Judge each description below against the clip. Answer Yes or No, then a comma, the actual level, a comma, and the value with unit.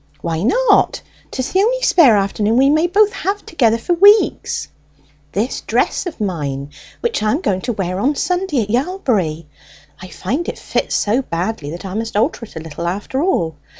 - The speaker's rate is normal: Yes, average, 185 wpm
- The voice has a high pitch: Yes, high, 225 Hz